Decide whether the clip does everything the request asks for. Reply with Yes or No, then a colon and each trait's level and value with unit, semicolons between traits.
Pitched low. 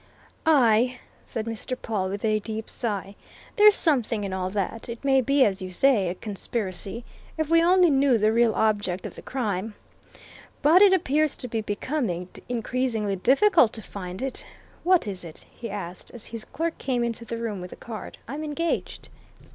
No: high, 230 Hz